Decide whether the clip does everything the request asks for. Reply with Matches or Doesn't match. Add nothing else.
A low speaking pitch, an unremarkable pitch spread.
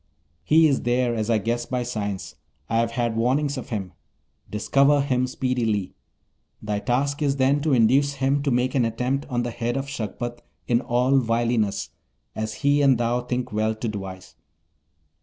Matches